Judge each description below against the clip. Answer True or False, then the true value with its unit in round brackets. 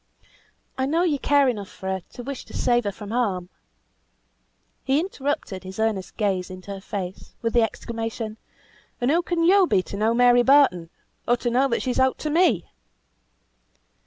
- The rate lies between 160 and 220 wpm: True (180 wpm)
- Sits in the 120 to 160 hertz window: False (235 Hz)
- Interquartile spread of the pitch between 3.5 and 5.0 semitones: False (5.6 semitones)